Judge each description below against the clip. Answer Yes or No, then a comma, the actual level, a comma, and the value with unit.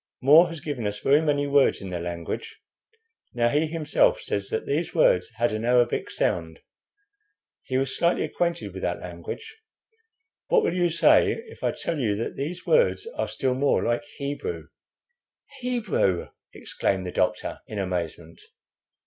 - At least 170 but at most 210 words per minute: No, average, 155 wpm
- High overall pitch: No, low, 135 Hz